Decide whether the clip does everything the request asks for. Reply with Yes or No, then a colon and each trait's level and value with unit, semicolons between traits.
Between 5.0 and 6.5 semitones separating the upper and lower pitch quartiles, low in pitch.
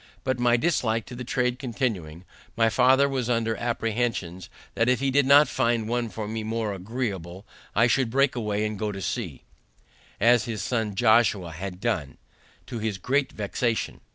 No: average, 3.0 semitones; low, 115 Hz